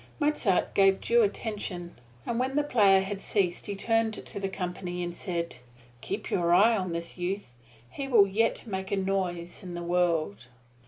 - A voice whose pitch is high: Yes, high, 195 Hz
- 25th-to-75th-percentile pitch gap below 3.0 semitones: No, average, 3.4 semitones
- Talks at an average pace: Yes, average, 175 wpm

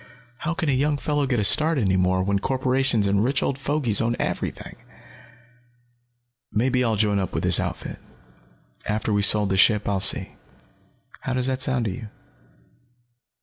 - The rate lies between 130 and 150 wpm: No, average, 170 wpm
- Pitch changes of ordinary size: Yes, average, 4.7 semitones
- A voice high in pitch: No, low, 120 Hz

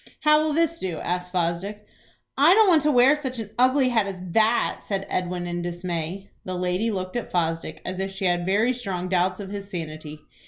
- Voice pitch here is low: No, high, 195 Hz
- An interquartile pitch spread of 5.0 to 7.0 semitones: Yes, wide, 5.5 semitones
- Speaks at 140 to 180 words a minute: No, fast, 205 wpm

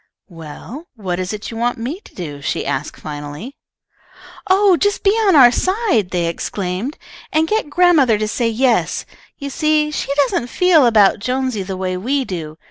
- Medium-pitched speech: No, high, 240 Hz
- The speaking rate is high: No, average, 175 wpm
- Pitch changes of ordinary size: No, wide, 8.7 semitones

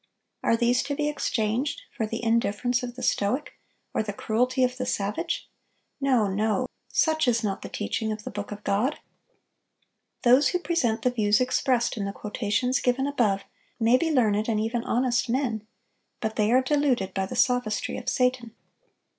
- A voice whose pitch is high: Yes, high, 240 Hz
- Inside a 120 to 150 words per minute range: No, average, 175 wpm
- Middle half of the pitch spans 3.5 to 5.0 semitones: No, average, 3.1 semitones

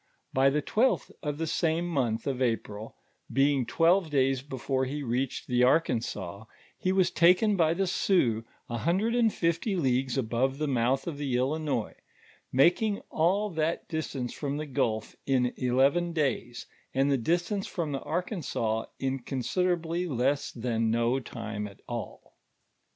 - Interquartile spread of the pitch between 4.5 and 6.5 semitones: Yes, wide, 5.4 semitones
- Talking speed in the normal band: Yes, average, 155 wpm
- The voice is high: No, medium, 140 Hz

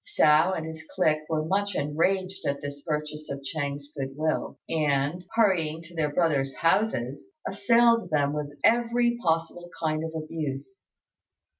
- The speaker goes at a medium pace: Yes, average, 145 wpm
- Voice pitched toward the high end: No, medium, 155 Hz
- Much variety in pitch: No, average, 4.0 semitones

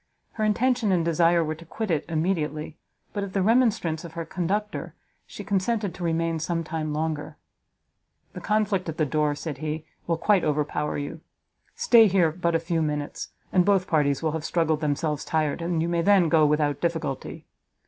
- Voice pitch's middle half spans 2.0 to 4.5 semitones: Yes, average, 3.5 semitones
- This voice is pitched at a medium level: Yes, medium, 165 Hz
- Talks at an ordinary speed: Yes, average, 185 wpm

